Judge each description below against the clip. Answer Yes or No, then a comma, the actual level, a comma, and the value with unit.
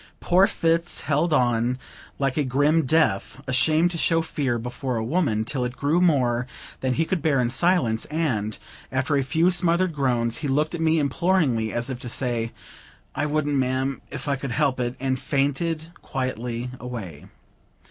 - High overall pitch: No, low, 135 Hz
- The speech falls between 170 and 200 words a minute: Yes, average, 175 wpm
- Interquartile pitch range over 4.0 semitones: Yes, average, 4.5 semitones